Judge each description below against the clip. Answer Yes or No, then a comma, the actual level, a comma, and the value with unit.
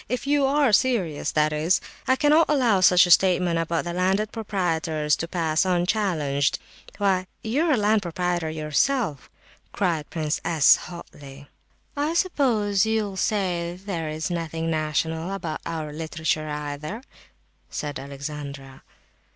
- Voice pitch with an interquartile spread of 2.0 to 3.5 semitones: No, average, 5.0 semitones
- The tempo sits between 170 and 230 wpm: No, slow, 135 wpm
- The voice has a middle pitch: Yes, medium, 175 Hz